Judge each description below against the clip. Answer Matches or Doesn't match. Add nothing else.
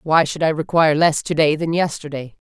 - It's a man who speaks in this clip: Doesn't match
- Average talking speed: Doesn't match